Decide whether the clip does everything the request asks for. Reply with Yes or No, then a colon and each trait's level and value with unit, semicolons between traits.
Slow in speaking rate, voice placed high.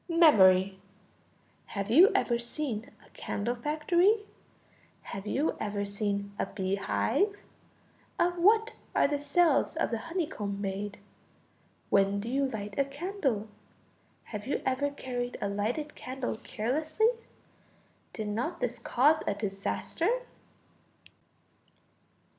Yes: slow, 120 wpm; high, 245 Hz